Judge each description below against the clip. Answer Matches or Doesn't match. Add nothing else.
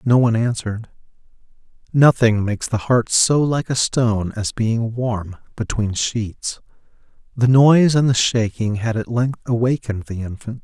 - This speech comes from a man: Matches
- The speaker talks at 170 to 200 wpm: Doesn't match